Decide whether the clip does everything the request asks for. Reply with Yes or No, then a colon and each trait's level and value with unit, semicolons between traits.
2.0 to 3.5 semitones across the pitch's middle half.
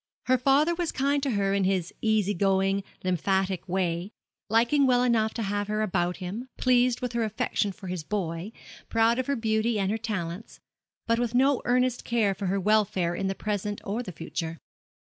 No: average, 3.9 semitones